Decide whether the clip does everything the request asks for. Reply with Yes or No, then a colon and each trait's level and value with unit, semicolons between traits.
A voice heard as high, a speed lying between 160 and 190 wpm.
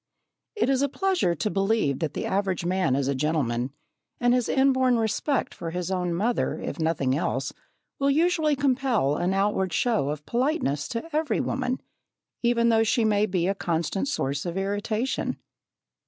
Yes: high, 205 Hz; average, 170 wpm